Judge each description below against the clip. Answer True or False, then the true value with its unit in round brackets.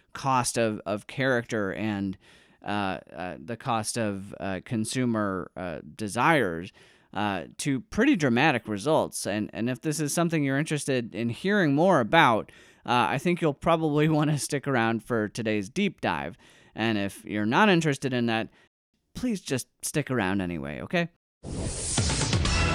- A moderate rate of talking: True (150 wpm)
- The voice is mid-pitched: False (120 Hz)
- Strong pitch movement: True (6.0 semitones)